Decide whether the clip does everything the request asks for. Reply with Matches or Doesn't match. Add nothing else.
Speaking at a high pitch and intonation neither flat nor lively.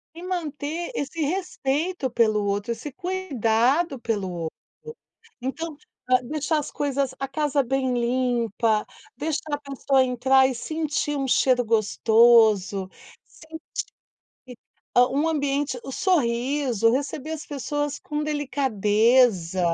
Matches